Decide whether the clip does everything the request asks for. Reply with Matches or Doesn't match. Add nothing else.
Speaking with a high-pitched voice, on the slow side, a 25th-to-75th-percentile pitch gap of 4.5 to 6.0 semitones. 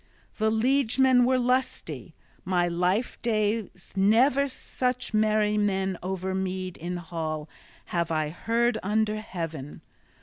Matches